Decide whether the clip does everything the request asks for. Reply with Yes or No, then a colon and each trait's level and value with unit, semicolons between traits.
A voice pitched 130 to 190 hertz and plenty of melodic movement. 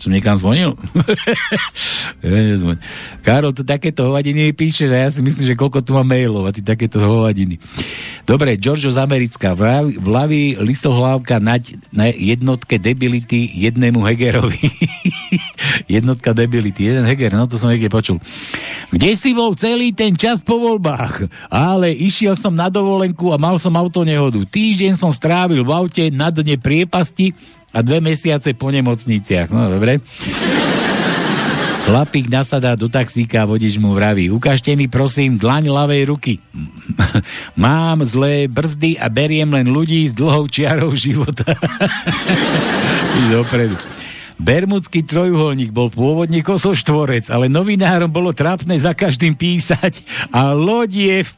Yes: medium, 140 Hz; wide, 5.8 semitones